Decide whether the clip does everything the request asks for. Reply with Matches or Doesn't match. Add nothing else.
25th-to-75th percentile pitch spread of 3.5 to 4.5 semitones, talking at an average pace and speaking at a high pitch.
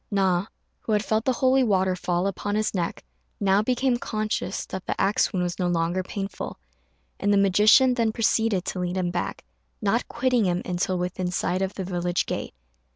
Doesn't match